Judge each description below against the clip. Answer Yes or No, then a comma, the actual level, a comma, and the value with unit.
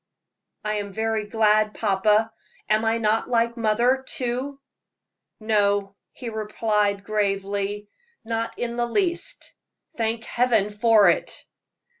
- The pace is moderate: No, slow, 115 wpm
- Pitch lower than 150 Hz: No, high, 220 Hz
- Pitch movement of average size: No, narrow, 1.9 semitones